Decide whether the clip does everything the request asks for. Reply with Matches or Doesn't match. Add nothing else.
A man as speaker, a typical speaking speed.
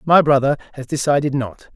Matches